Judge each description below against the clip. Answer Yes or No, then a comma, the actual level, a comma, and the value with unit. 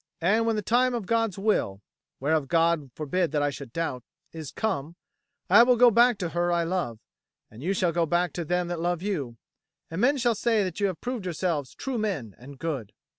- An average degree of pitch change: No, wide, 5.8 semitones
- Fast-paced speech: Yes, fast, 215 wpm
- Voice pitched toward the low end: No, medium, 175 Hz